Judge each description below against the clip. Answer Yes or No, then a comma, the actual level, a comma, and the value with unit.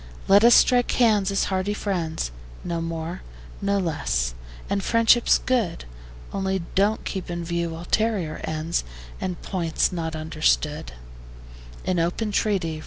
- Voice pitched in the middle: Yes, medium, 180 Hz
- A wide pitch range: No, average, 3.7 semitones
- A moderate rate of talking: No, slow, 130 wpm